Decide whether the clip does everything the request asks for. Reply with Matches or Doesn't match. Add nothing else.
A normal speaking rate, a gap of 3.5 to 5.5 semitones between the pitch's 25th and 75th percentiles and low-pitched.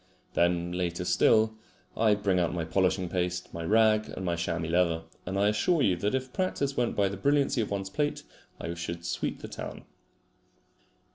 Matches